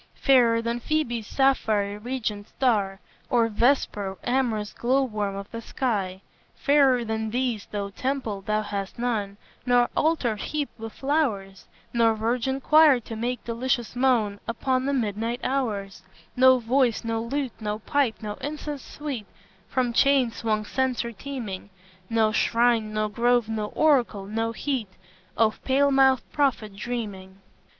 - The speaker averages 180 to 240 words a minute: No, average, 140 wpm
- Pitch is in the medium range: No, high, 235 Hz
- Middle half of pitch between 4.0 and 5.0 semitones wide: No, average, 3.6 semitones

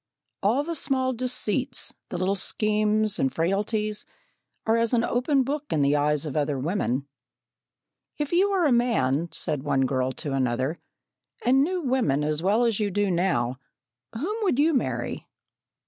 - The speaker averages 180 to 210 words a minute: No, average, 160 wpm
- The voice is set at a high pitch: Yes, high, 210 Hz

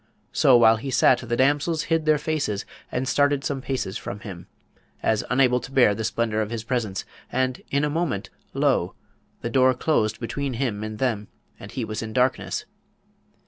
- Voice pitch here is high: No, low, 125 Hz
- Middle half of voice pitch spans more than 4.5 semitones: No, average, 4.0 semitones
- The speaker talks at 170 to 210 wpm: Yes, average, 185 wpm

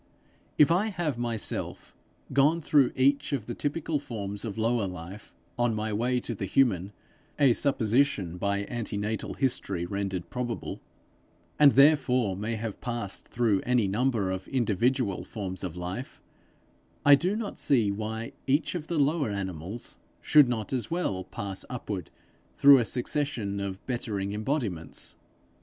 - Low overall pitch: Yes, low, 115 Hz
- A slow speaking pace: No, average, 145 wpm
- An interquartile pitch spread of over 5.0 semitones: Yes, wide, 5.4 semitones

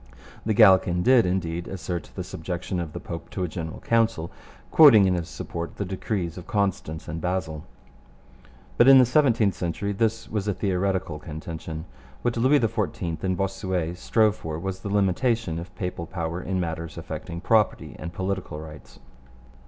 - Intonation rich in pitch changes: No, average, 3.7 semitones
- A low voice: Yes, very low, 95 Hz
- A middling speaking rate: Yes, average, 165 wpm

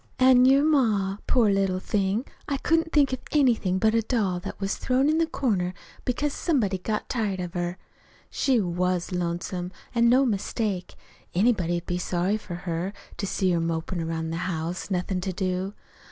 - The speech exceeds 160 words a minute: Yes, average, 175 wpm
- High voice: Yes, high, 195 Hz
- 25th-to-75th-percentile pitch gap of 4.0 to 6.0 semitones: Yes, wide, 5.4 semitones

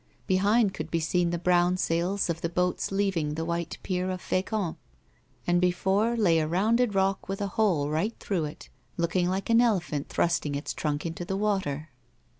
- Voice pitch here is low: No, medium, 180 Hz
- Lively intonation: No, average, 2.9 semitones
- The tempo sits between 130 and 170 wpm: No, average, 185 wpm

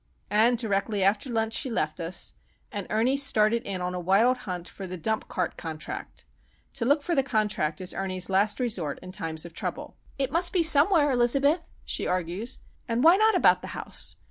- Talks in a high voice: Yes, high, 215 Hz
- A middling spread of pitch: No, wide, 6.1 semitones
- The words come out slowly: No, average, 195 wpm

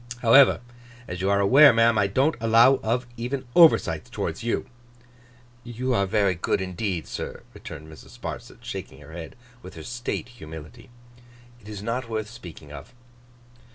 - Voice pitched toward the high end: No, low, 110 Hz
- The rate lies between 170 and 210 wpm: No, average, 155 wpm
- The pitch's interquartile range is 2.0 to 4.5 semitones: No, average, 5.1 semitones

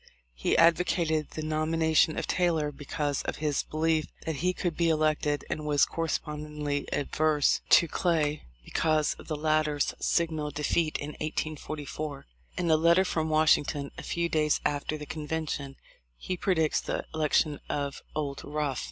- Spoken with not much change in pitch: Yes, narrow, 1.5 semitones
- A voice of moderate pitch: Yes, medium, 155 Hz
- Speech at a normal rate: Yes, average, 150 wpm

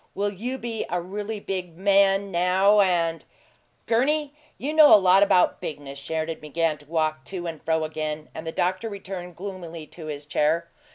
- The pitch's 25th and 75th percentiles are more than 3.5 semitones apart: Yes, average, 3.9 semitones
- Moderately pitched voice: Yes, medium, 180 Hz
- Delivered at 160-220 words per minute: Yes, average, 180 wpm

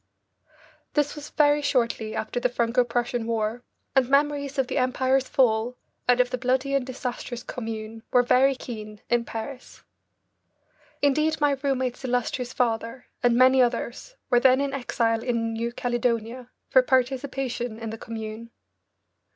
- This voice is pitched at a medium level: No, high, 245 Hz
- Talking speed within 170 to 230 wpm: No, average, 145 wpm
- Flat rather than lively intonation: Yes, narrow, 2.3 semitones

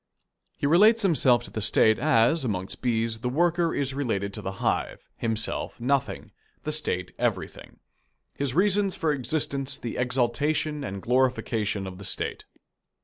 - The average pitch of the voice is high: No, low, 130 Hz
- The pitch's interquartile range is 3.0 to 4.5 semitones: No, average, 5.3 semitones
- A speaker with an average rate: Yes, average, 145 wpm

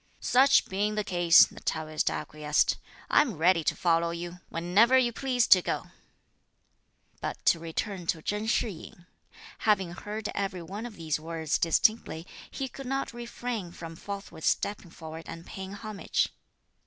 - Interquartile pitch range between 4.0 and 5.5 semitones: Yes, average, 4.7 semitones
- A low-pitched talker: No, high, 190 Hz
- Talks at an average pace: Yes, average, 155 wpm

